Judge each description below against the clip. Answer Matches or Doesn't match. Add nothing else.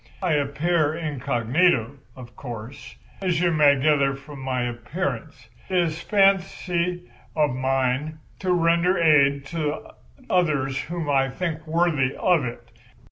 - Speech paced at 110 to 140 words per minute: Matches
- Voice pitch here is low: Doesn't match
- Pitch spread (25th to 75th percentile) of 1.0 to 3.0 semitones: Doesn't match